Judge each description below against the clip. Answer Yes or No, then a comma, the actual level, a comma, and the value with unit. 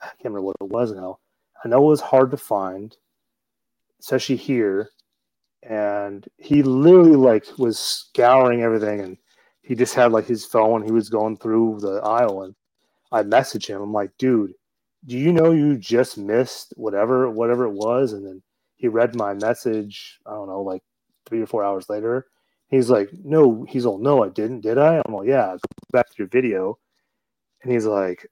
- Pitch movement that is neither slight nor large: Yes, average, 4.0 semitones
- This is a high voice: No, low, 115 Hz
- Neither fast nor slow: Yes, average, 190 wpm